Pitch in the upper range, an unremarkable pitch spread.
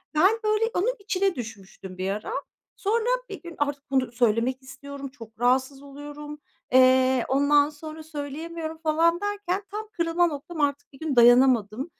Yes: very high, 290 Hz; average, 4.6 semitones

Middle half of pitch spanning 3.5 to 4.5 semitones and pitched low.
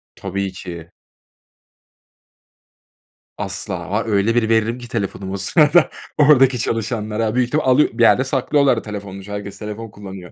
Yes: average, 4.0 semitones; low, 110 Hz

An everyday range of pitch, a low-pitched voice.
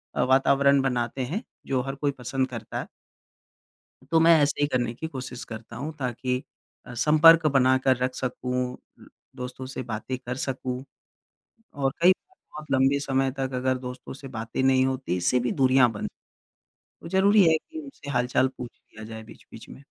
No: narrow, 2.0 semitones; low, 130 Hz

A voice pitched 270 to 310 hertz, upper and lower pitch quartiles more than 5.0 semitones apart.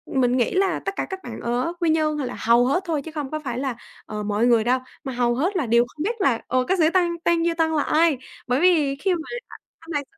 Yes: very high, 295 Hz; wide, 5.4 semitones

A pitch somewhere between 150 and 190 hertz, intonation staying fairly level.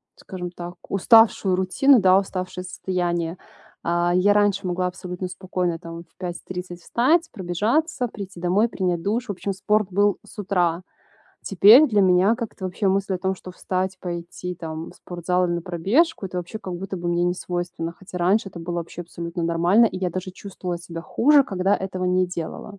Yes: medium, 185 Hz; narrow, 2.3 semitones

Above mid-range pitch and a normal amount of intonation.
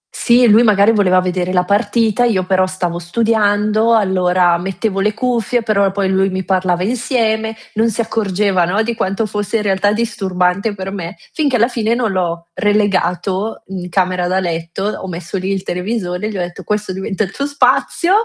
Yes: high, 200 Hz; average, 3.2 semitones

